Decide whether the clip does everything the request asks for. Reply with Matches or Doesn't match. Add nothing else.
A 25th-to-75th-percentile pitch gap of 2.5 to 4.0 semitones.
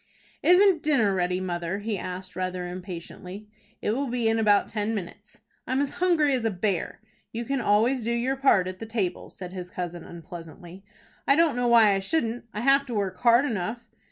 Doesn't match